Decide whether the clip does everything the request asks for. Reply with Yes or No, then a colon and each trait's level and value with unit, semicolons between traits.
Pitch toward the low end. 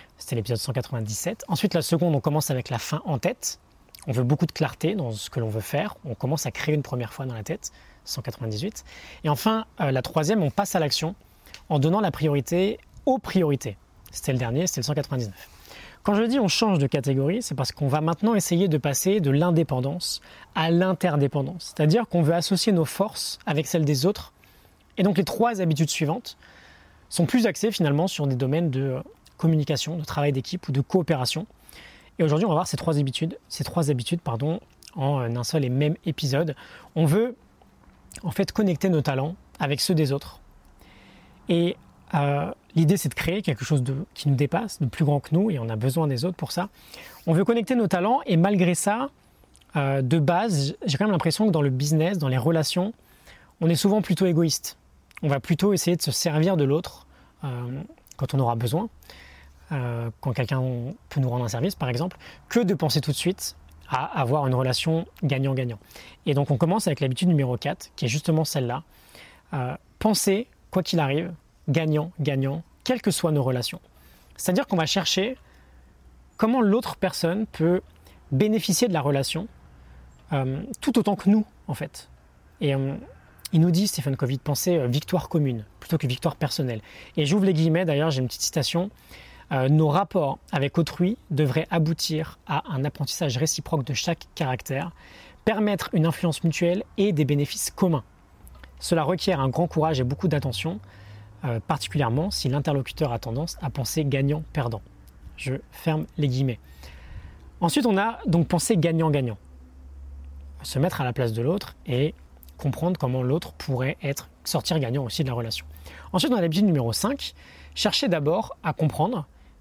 No: medium, 150 Hz